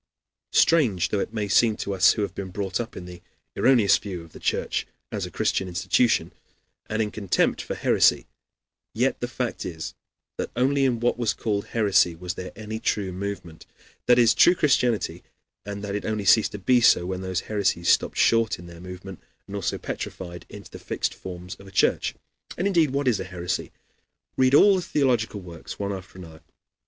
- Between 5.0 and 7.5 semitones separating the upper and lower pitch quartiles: No, average, 4.2 semitones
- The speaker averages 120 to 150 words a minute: No, average, 195 wpm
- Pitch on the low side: Yes, low, 100 Hz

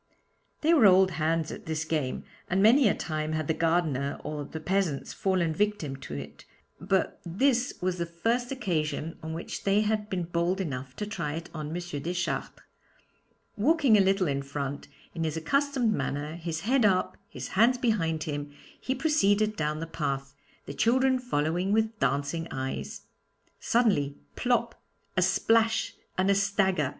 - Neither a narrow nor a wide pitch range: No, wide, 5.9 semitones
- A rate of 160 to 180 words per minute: Yes, average, 165 wpm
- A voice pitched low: No, medium, 175 Hz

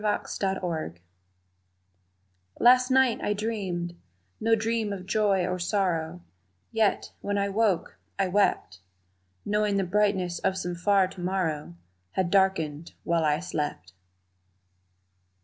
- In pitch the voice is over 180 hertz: Yes, high, 190 Hz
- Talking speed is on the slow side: Yes, slow, 115 wpm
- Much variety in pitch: No, average, 3.1 semitones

